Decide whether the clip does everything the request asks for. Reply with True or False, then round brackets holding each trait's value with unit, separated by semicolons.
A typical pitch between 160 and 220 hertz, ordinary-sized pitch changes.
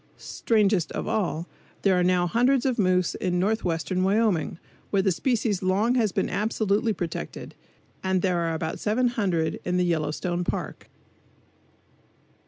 True (190 Hz; 3.6 semitones)